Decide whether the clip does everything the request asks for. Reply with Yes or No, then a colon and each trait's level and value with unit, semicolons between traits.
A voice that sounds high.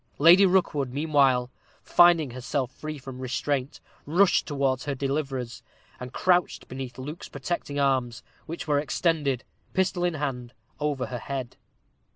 No: medium, 140 Hz